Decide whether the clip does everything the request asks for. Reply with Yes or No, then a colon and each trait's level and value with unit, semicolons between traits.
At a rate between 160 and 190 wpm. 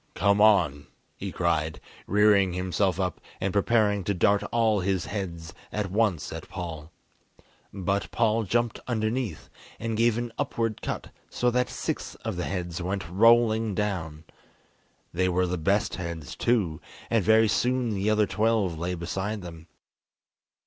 No: average, 150 wpm